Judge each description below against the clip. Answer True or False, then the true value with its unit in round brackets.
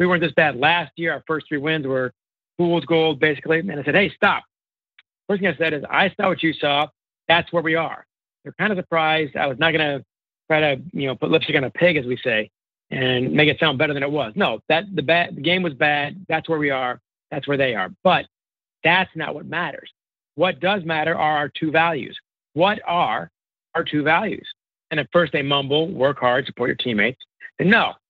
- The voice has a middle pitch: True (155 Hz)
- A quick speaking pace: True (230 wpm)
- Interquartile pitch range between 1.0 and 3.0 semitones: True (2.7 semitones)